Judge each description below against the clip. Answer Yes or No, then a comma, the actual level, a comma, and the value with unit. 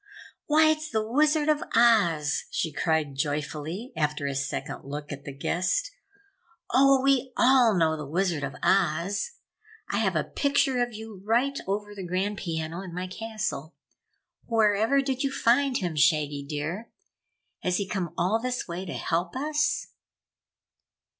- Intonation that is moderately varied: No, wide, 8.0 semitones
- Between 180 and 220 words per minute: No, average, 155 wpm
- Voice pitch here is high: Yes, high, 195 Hz